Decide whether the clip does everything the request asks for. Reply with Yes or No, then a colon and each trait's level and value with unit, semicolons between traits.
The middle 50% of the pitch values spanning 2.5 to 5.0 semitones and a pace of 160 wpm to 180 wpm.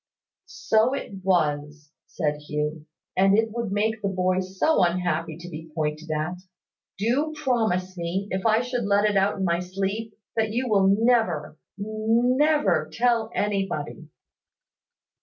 No: average, 4.7 semitones; average, 140 wpm